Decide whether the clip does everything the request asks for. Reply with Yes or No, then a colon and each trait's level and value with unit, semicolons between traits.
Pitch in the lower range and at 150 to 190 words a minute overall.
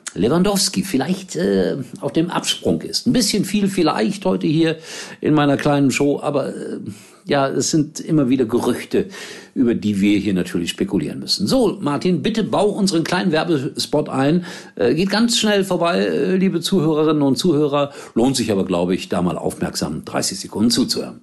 No: medium, 160 Hz; average, 170 wpm